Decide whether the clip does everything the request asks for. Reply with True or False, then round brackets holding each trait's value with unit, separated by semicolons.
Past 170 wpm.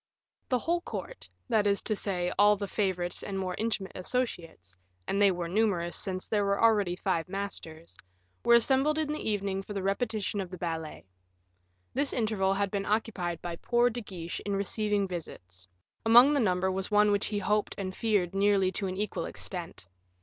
True (190 wpm)